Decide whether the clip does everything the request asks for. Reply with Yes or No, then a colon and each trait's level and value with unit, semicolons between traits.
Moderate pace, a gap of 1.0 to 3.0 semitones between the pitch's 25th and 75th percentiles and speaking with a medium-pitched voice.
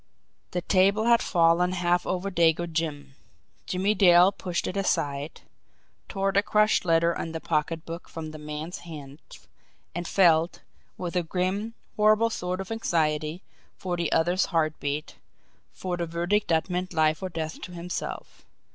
Yes: average, 150 wpm; narrow, 2.6 semitones; medium, 175 Hz